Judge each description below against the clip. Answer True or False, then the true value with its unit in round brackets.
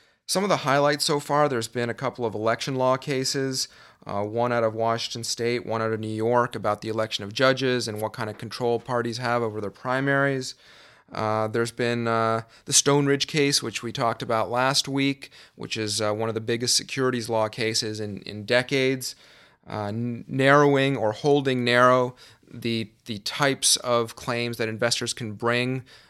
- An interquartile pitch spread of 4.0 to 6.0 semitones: False (2.8 semitones)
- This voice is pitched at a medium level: False (120 Hz)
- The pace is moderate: True (185 wpm)